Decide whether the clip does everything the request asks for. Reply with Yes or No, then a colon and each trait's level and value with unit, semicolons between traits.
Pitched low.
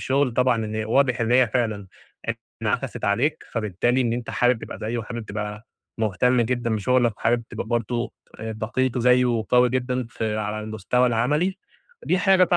Yes: low, 120 Hz